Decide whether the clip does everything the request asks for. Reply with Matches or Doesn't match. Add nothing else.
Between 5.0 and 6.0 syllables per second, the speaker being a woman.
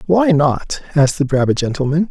Doesn't match